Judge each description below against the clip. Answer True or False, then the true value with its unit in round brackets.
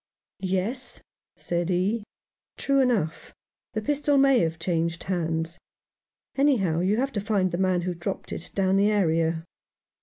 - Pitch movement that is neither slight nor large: True (4.7 semitones)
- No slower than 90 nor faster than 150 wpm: True (145 wpm)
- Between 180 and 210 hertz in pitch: True (185 Hz)